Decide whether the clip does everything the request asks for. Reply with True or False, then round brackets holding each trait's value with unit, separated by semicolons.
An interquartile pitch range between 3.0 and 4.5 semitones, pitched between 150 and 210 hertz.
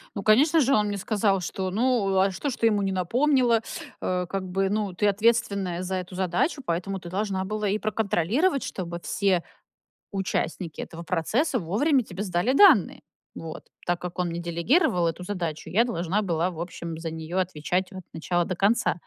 True (3.5 semitones; 190 Hz)